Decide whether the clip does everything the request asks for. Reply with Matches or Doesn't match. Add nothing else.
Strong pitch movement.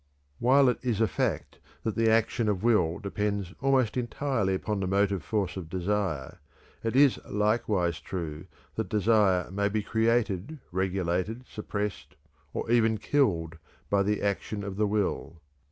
Doesn't match